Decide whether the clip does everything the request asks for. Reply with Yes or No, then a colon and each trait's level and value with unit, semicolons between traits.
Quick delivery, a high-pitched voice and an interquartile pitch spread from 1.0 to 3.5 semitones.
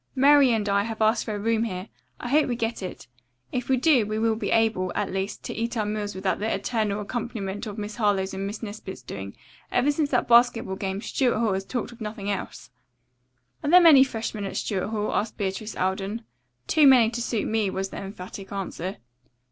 Yes: fast, 210 wpm; high, 215 Hz; average, 3.1 semitones